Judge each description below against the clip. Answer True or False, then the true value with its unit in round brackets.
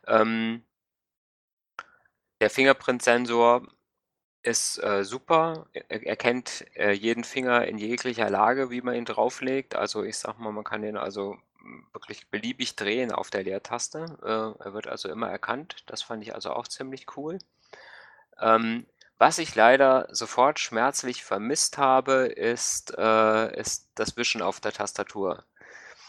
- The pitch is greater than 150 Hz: False (120 Hz)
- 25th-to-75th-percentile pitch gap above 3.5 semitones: False (3.2 semitones)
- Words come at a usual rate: True (140 wpm)